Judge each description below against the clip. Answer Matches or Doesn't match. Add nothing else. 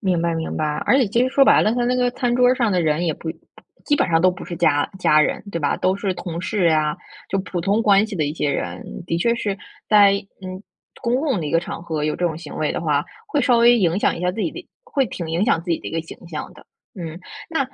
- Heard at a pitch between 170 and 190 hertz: Matches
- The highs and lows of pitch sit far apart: Matches